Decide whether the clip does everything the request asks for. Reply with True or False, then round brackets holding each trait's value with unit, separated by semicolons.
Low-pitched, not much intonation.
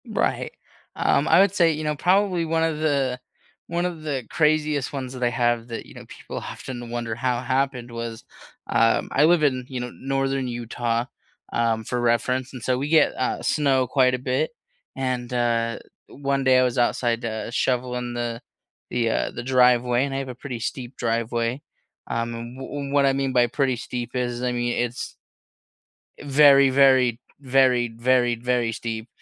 True (125 Hz; 2.3 semitones)